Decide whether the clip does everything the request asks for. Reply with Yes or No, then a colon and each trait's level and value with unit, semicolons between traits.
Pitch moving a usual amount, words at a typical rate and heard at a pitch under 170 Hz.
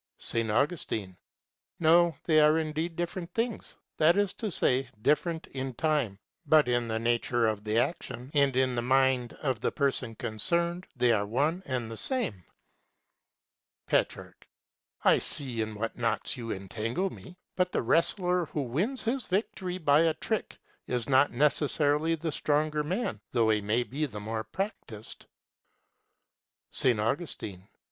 No: wide, 6.2 semitones; average, 150 wpm; medium, 140 Hz